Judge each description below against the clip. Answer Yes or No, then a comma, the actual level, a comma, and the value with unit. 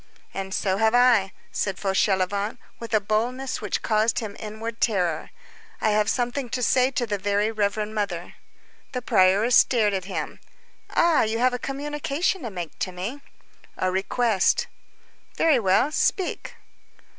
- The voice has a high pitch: Yes, high, 215 Hz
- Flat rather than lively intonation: No, average, 4.1 semitones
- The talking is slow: No, average, 150 wpm